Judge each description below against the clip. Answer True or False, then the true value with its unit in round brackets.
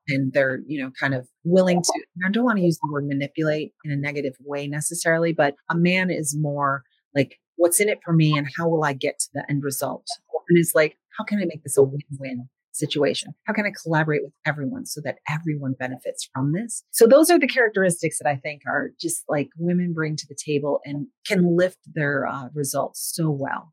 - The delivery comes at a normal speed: False (225 wpm)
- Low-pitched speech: False (150 Hz)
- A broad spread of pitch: False (3.4 semitones)